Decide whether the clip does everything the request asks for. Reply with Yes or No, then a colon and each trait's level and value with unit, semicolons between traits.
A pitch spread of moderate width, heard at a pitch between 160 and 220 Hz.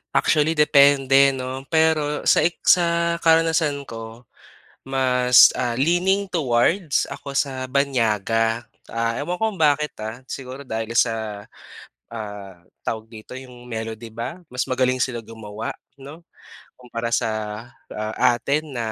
No: average, 4.7 semitones; low, 130 Hz